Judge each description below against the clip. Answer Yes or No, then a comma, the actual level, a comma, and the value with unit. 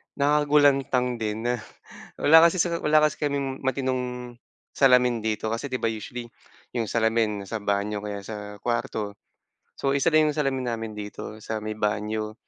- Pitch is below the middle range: Yes, low, 120 Hz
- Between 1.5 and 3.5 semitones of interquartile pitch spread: No, average, 4.2 semitones